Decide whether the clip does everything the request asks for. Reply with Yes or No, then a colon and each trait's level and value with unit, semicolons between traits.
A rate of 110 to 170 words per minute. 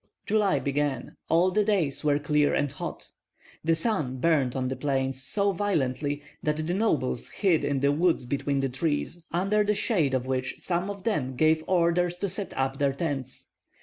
No: average, 180 wpm